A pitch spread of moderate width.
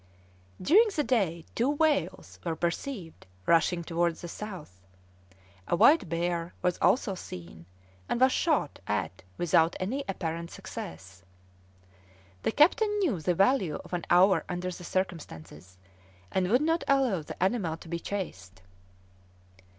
No: wide, 6.2 semitones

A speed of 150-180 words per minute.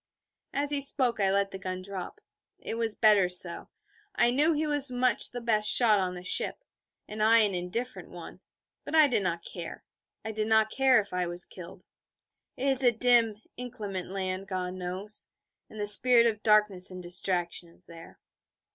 No: average, 190 wpm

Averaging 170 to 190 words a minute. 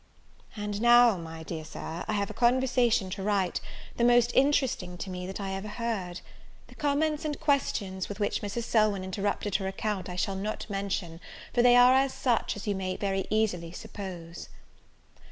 Yes: average, 175 wpm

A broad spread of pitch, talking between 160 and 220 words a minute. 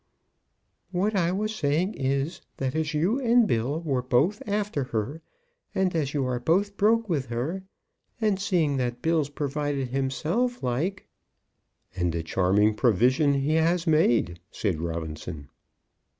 No: wide, 7.0 semitones; average, 145 wpm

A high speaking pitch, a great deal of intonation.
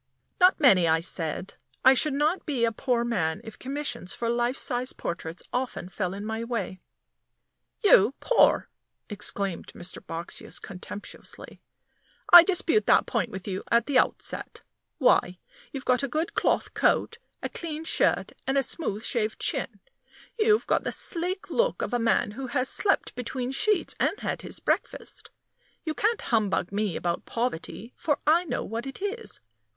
Yes: high, 245 Hz; wide, 7.1 semitones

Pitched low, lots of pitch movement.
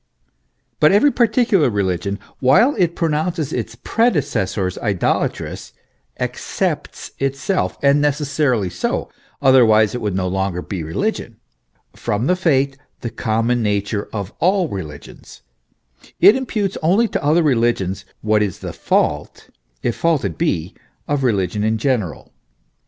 Yes: low, 125 Hz; wide, 7.9 semitones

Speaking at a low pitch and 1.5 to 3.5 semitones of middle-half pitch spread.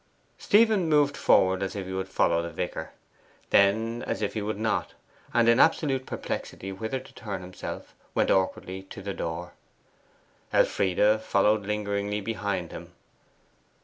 Yes: low, 100 Hz; average, 3.1 semitones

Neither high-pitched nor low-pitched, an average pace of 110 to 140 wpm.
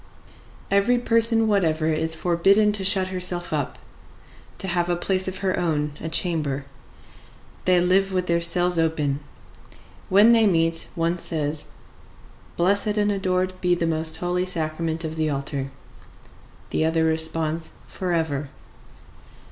Yes: medium, 175 Hz; slow, 135 wpm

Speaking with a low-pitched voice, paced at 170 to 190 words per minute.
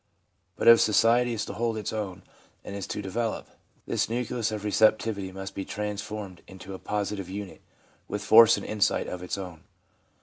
Yes: low, 105 Hz; average, 175 wpm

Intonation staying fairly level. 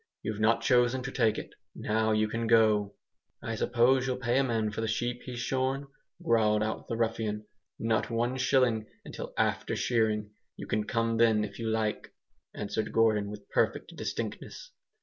Yes: narrow, 2.2 semitones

